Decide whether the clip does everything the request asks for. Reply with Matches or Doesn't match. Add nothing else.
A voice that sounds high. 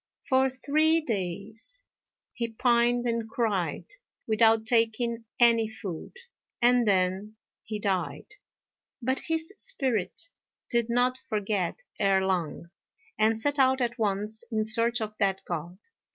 Matches